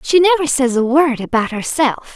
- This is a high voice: Yes, very high, 270 Hz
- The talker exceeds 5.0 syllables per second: No, 4.9 syllables/s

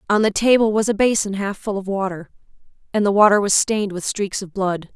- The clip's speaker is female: Yes, female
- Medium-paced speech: No, fast, 230 wpm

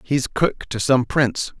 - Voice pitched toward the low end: Yes, low, 130 Hz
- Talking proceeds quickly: No, average, 190 wpm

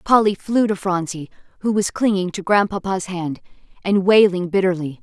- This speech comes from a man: No, female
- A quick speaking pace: No, average, 155 wpm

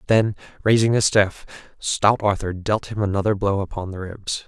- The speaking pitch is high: No, low, 100 Hz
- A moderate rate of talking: Yes, average, 175 wpm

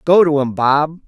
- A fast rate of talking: Yes, fast, 225 wpm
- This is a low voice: No, medium, 150 Hz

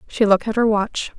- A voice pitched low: No, high, 215 Hz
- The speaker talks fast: Yes, fast, 255 wpm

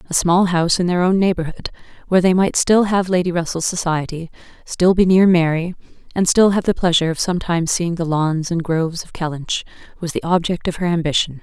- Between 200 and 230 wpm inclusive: Yes, fast, 205 wpm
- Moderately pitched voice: Yes, medium, 175 Hz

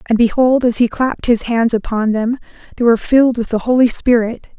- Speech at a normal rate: No, fast, 210 wpm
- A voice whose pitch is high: Yes, high, 235 Hz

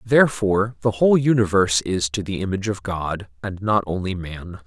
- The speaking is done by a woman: No, male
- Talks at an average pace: Yes, average, 180 wpm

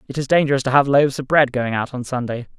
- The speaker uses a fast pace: Yes, fast, 280 wpm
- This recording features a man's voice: Yes, male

